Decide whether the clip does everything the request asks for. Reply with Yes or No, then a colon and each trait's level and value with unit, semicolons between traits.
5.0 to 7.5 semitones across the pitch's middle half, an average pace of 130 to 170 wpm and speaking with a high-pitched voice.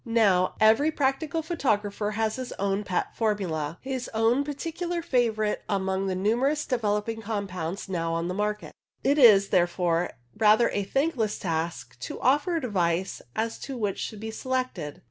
Yes: average, 5.3 semitones; average, 150 wpm; high, 215 Hz